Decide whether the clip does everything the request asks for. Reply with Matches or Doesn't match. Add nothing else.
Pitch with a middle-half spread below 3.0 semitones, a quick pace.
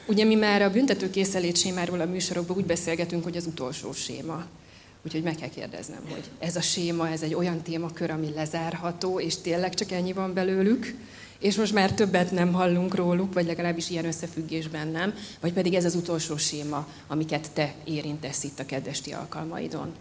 Matches